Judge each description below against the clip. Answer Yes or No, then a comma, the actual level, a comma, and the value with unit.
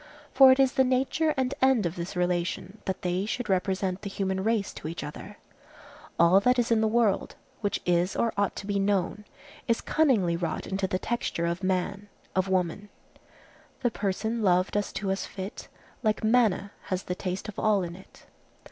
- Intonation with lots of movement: No, average, 3.5 semitones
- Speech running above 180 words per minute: Yes, average, 190 wpm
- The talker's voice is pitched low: No, high, 195 Hz